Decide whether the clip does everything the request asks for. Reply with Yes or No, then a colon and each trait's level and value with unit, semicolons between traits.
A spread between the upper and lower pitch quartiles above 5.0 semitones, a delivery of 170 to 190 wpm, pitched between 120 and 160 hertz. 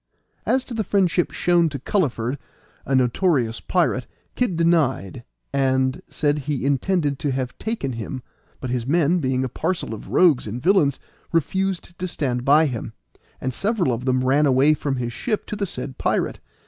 Yes: wide, 5.4 semitones; average, 175 wpm; medium, 140 Hz